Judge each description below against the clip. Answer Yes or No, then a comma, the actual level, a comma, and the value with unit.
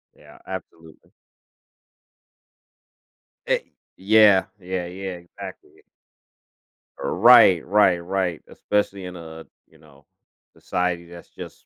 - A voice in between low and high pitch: No, very low, 90 Hz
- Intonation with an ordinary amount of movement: No, narrow, 2.2 semitones